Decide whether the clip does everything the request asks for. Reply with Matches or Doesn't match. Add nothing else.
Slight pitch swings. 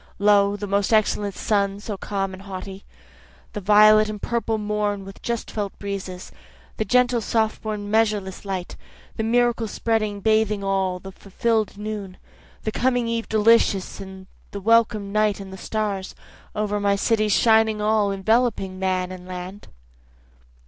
Matches